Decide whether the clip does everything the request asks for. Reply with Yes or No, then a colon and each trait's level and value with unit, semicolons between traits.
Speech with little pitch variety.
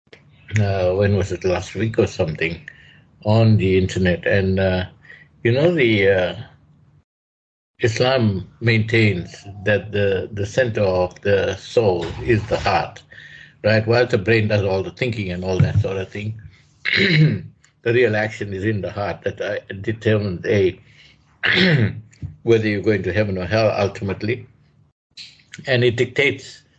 No: average, 3.5 semitones